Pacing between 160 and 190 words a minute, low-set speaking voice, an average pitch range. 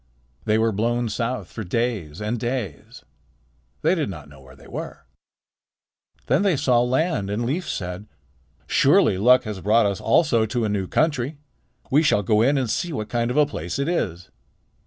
Yes: average, 180 wpm; low, 115 Hz; average, 4.3 semitones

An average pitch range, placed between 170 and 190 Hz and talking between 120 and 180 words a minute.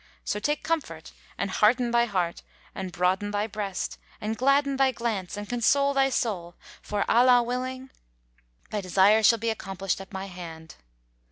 No: average, 4.5 semitones; high, 215 Hz; average, 160 wpm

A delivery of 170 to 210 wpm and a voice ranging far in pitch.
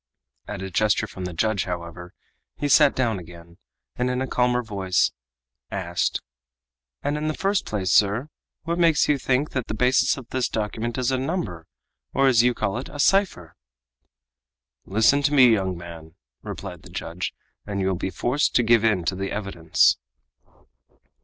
Yes: average, 175 wpm; wide, 6.0 semitones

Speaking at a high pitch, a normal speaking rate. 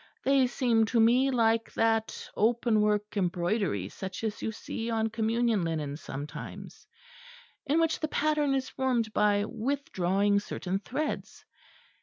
No: high, 225 Hz; slow, 130 wpm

